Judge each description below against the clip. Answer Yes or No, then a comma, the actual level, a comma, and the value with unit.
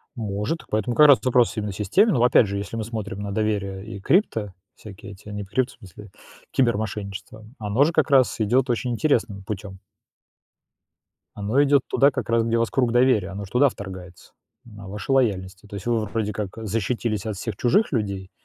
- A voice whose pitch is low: Yes, low, 110 Hz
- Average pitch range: Yes, average, 3.4 semitones